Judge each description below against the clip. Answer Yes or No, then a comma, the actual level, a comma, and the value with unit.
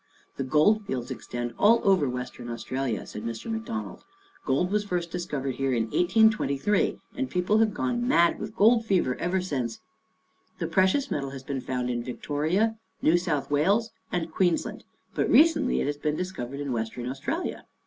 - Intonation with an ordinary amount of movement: No, wide, 8.0 semitones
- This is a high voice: No, medium, 170 Hz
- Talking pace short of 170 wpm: No, average, 180 wpm